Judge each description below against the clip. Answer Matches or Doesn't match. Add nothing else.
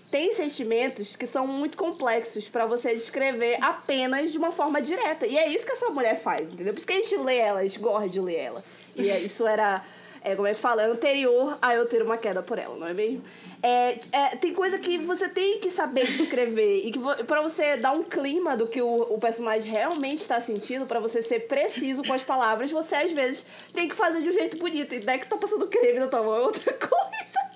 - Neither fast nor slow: Doesn't match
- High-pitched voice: Matches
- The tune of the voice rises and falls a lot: Matches